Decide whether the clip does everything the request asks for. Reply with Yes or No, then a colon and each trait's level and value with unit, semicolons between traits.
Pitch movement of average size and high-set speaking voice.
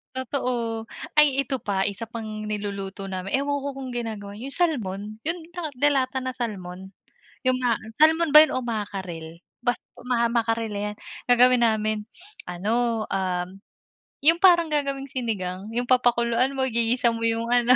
Yes: average, 4.0 semitones; high, 235 Hz